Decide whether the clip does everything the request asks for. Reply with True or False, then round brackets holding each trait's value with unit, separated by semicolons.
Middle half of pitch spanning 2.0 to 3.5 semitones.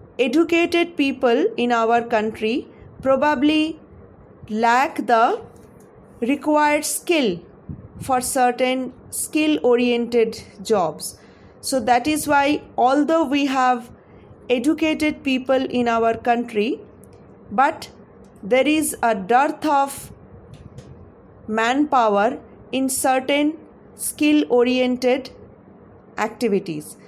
False (4.0 semitones)